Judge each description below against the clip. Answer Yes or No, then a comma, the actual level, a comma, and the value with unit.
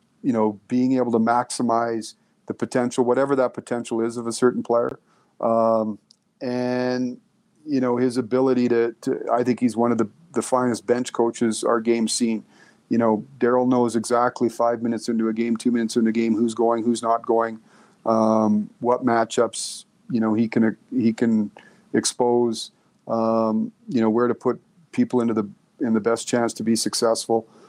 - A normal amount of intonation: No, narrow, 1.4 semitones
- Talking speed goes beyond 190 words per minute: No, average, 180 wpm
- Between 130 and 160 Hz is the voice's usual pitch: No, low, 115 Hz